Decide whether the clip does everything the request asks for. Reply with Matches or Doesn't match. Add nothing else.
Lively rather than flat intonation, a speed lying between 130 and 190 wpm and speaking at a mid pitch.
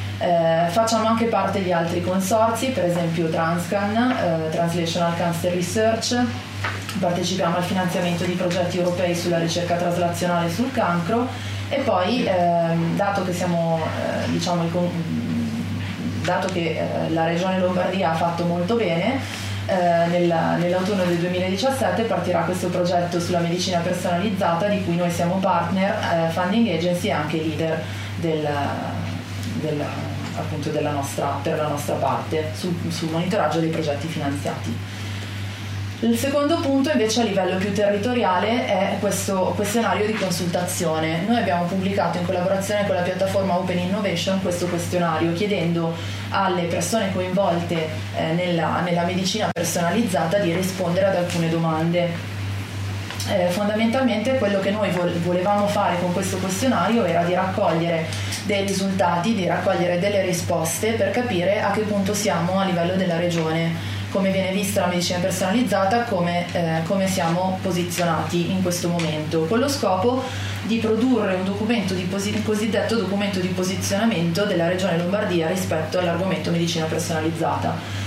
Doesn't match